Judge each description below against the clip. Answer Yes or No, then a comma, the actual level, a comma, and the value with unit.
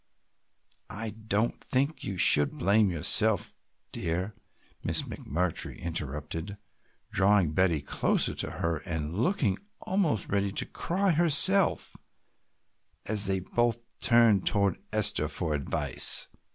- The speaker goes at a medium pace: No, slow, 110 wpm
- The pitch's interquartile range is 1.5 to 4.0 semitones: No, wide, 5.4 semitones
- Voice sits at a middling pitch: No, low, 100 Hz